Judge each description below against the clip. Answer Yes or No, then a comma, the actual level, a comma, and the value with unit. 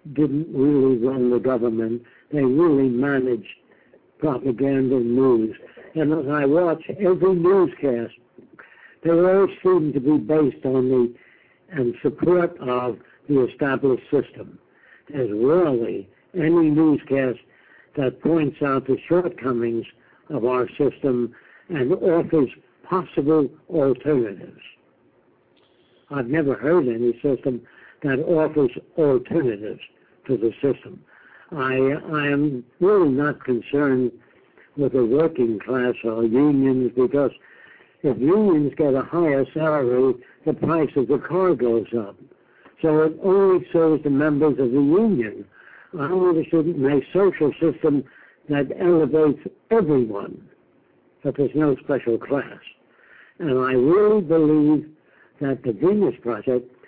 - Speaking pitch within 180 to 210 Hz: No, medium, 140 Hz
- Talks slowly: Yes, slow, 120 wpm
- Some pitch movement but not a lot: Yes, average, 4.0 semitones